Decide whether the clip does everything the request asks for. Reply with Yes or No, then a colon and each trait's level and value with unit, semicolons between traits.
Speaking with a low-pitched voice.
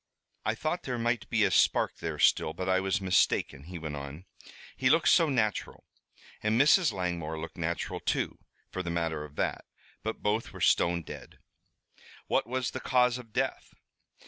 Yes: very low, 95 Hz